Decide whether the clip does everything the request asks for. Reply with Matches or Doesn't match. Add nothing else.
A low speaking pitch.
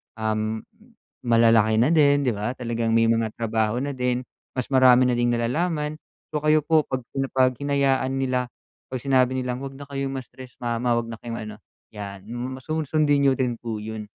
Matches